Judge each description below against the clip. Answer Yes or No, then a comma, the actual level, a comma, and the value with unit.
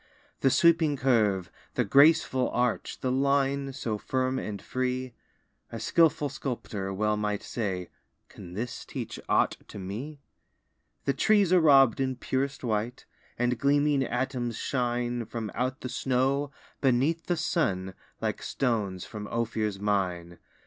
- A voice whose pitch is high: No, low, 125 Hz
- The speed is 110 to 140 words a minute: Yes, slow, 135 wpm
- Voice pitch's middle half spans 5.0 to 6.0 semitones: No, average, 4.4 semitones